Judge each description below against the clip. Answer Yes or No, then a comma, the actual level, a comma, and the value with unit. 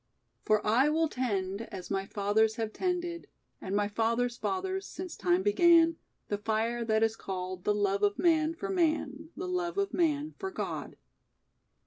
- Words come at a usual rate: Yes, average, 165 wpm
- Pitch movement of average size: No, wide, 8.5 semitones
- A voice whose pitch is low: No, high, 235 Hz